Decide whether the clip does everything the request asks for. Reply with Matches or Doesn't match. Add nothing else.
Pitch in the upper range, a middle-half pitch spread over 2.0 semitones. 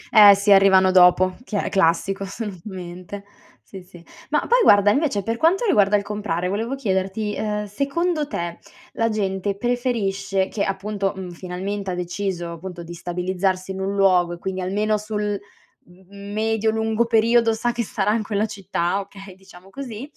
Matches